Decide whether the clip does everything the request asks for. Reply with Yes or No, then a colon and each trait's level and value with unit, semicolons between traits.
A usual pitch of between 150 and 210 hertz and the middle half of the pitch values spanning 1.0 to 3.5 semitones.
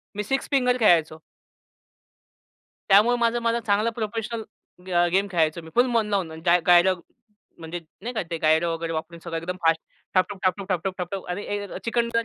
No: high, 190 Hz; average, 5.3 semitones